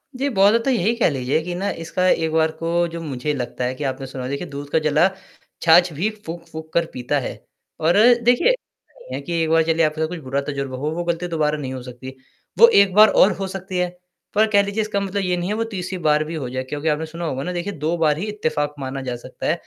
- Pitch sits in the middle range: Yes, medium, 160 Hz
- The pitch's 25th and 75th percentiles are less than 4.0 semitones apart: No, average, 4.3 semitones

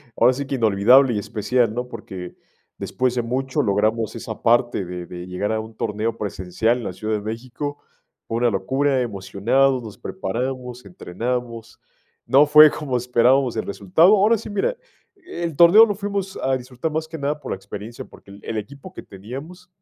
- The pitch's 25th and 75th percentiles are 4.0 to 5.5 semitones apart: Yes, average, 4.7 semitones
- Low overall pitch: Yes, low, 125 Hz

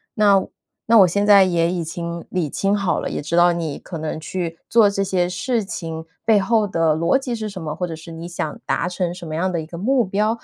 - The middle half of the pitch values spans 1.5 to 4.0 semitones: Yes, average, 3.5 semitones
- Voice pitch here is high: No, medium, 180 Hz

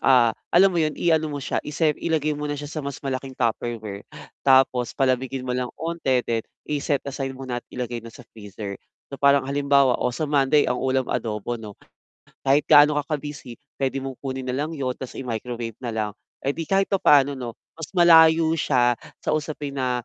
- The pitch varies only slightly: No, average, 3.2 semitones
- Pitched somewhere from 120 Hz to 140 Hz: Yes, low, 135 Hz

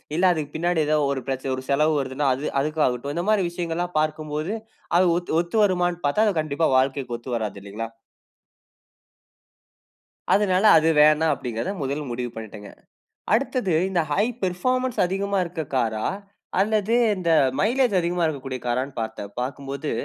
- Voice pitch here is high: No, medium, 155 Hz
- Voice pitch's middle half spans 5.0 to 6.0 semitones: Yes, wide, 5.4 semitones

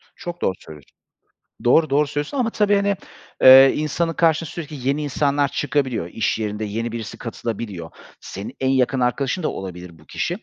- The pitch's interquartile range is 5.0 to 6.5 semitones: Yes, wide, 5.4 semitones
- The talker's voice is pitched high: No, low, 135 Hz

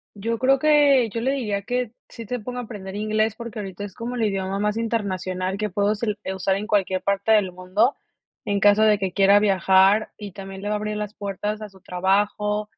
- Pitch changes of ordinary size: No, narrow, 2.3 semitones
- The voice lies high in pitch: Yes, high, 210 Hz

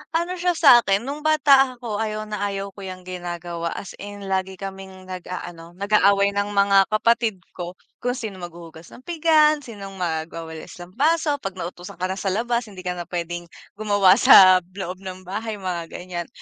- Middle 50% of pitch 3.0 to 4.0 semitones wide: Yes, average, 3.6 semitones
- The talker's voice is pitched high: Yes, high, 195 Hz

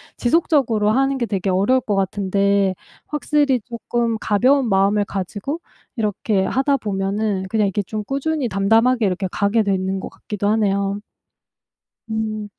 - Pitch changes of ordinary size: Yes, average, 3.6 semitones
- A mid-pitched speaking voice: No, high, 210 Hz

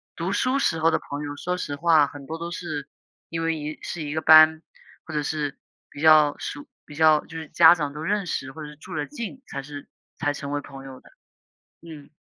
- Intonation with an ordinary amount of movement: No, narrow, 2.1 semitones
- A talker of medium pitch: Yes, medium, 155 Hz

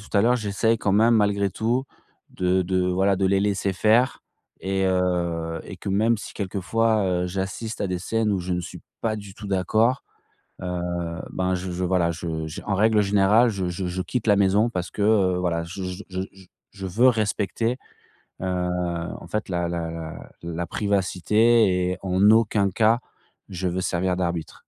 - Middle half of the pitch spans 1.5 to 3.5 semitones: Yes, average, 2.9 semitones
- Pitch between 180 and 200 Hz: No, very low, 95 Hz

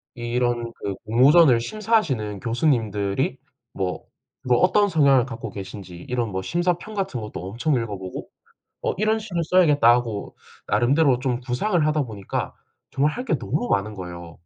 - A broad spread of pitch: Yes, wide, 7.1 semitones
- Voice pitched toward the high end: No, low, 125 Hz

